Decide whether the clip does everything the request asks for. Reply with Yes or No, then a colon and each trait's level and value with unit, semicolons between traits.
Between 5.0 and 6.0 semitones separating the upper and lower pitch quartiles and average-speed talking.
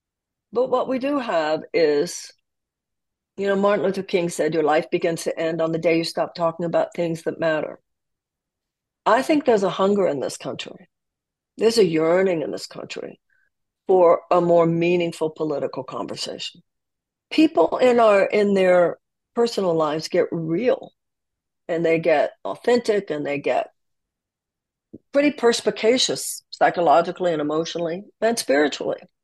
Yes: wide, 5.4 semitones; average, 145 wpm